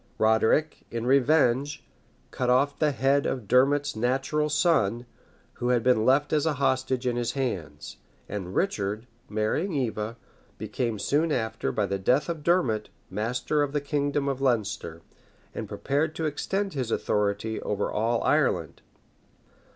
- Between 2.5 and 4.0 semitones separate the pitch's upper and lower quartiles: No, average, 4.7 semitones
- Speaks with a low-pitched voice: Yes, low, 125 Hz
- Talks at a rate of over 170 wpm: No, average, 145 wpm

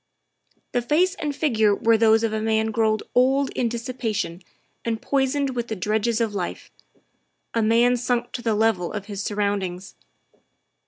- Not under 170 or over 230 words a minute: No, average, 160 wpm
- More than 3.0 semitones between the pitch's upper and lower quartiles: No, narrow, 2.6 semitones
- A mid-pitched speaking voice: No, high, 225 Hz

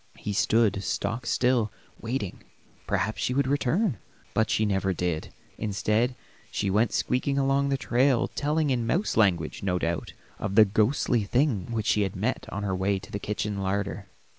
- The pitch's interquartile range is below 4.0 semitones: No, average, 4.4 semitones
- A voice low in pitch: Yes, low, 110 Hz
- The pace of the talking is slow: No, average, 170 wpm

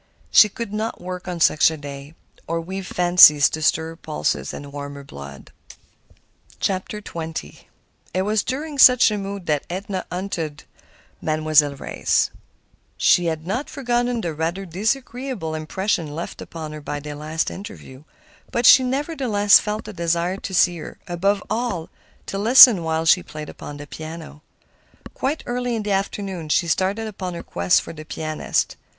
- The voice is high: No, medium, 175 Hz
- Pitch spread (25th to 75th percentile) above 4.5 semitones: Yes, average, 5.2 semitones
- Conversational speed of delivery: Yes, average, 160 wpm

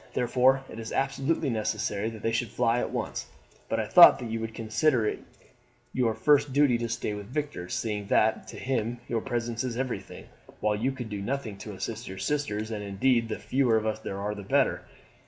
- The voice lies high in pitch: No, low, 115 Hz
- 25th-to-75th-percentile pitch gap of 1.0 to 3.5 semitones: Yes, average, 3.2 semitones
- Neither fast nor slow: No, fast, 210 wpm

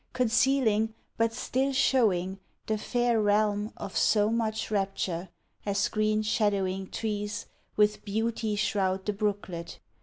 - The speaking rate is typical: No, slow, 120 wpm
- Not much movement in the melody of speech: Yes, narrow, 2.0 semitones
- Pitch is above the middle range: Yes, high, 210 Hz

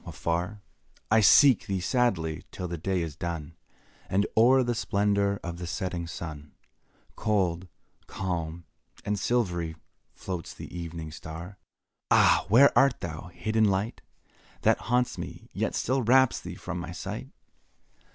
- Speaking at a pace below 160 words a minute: Yes, average, 150 wpm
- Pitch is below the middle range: Yes, very low, 95 Hz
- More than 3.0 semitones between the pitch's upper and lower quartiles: Yes, average, 4.5 semitones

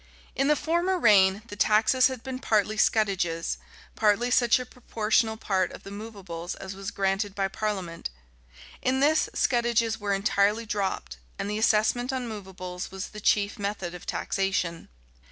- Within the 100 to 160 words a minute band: Yes, average, 155 wpm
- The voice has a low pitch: No, high, 210 Hz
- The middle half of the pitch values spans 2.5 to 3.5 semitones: Yes, average, 3.2 semitones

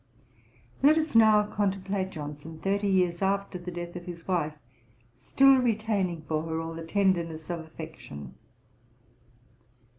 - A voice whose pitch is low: No, medium, 180 Hz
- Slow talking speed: Yes, slow, 130 wpm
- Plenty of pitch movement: No, average, 3.7 semitones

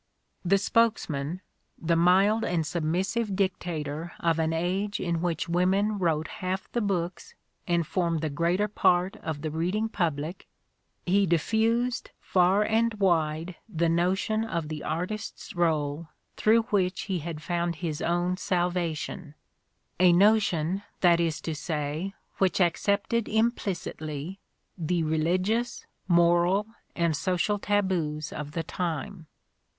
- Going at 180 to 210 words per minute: No, slow, 135 wpm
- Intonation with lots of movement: No, average, 3.4 semitones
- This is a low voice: No, medium, 175 Hz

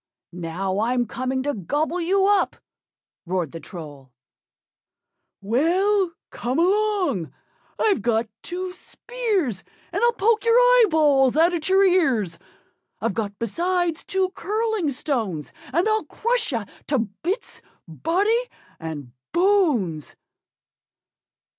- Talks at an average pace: No, slow, 115 wpm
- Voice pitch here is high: Yes, very high, 315 Hz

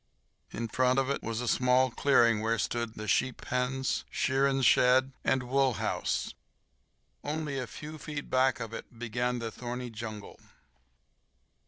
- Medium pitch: No, low, 125 Hz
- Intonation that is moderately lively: No, narrow, 2.3 semitones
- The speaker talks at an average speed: Yes, average, 150 wpm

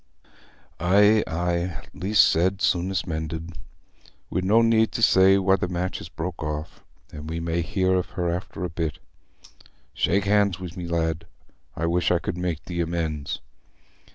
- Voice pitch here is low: Yes, very low, 90 Hz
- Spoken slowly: No, average, 160 wpm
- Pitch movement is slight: Yes, narrow, 2.3 semitones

